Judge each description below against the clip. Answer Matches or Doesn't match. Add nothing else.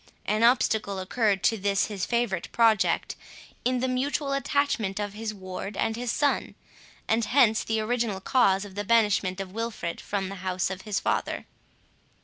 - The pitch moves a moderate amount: Matches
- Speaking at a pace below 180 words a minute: Matches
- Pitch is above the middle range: Matches